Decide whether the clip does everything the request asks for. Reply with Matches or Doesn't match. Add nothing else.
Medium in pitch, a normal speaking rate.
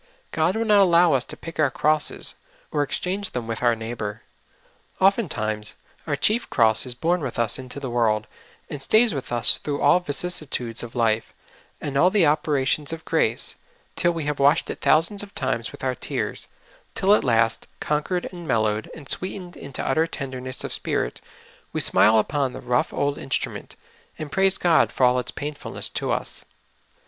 Matches